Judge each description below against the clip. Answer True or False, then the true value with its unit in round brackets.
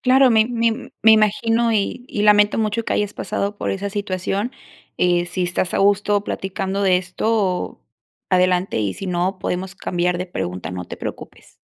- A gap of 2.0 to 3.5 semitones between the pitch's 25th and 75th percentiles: True (2.9 semitones)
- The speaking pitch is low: False (195 Hz)